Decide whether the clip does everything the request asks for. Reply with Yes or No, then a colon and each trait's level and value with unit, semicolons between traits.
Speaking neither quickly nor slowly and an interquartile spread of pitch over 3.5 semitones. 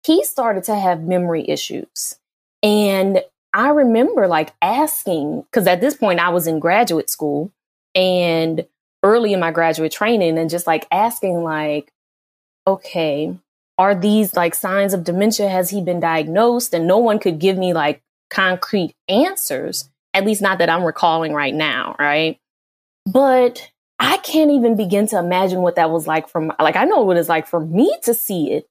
Yes: average, 175 wpm; average, 4.4 semitones